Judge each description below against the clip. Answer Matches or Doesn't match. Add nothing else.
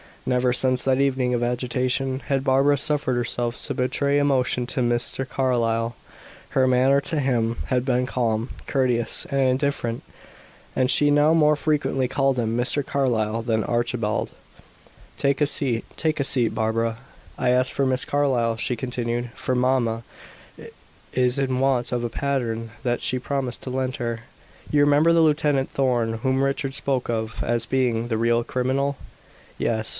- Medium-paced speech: Matches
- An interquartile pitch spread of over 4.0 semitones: Doesn't match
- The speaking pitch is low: Matches